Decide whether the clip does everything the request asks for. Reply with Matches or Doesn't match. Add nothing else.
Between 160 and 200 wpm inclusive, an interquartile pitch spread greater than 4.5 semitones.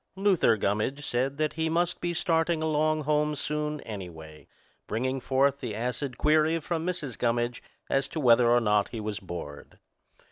Matches